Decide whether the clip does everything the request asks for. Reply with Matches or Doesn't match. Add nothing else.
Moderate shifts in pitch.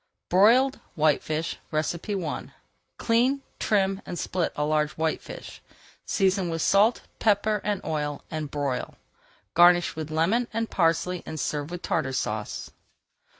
Matches